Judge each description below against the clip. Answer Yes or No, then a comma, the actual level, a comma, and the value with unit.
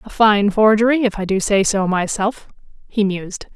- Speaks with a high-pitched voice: Yes, high, 205 Hz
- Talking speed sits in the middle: Yes, average, 185 wpm